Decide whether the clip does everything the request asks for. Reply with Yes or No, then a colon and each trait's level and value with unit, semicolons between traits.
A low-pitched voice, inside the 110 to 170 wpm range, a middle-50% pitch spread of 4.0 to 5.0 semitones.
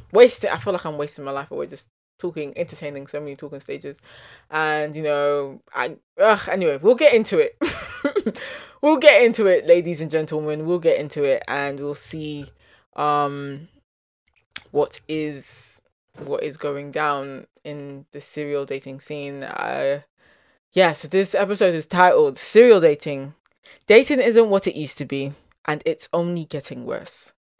No: medium, 150 Hz; average, 160 wpm; average, 4.3 semitones